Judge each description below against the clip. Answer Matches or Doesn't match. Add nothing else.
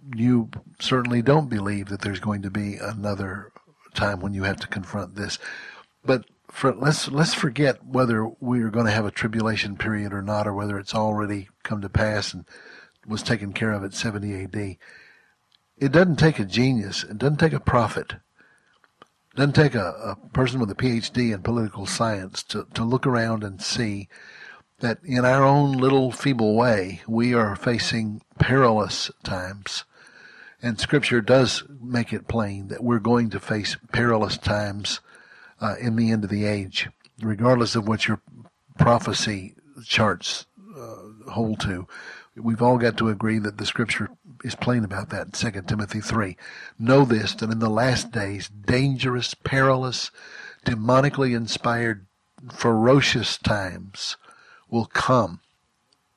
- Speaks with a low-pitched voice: Matches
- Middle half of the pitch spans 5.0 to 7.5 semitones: Doesn't match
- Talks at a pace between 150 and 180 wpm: Matches